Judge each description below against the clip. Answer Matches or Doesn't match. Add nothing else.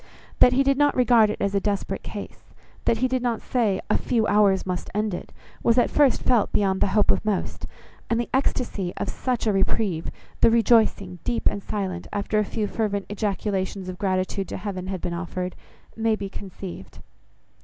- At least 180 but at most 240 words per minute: Matches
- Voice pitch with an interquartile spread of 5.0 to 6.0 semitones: Doesn't match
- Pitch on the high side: Matches